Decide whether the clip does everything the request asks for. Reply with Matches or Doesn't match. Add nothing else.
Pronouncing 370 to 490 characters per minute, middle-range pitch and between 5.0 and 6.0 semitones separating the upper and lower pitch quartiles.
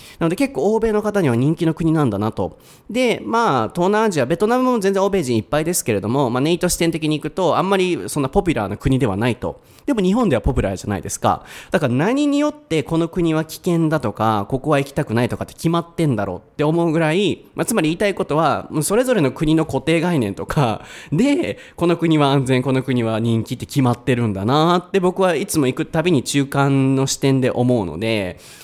Matches